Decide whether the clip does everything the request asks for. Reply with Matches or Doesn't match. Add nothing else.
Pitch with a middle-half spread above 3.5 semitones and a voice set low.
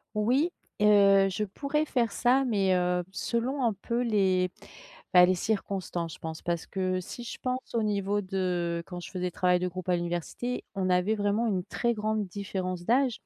Doesn't match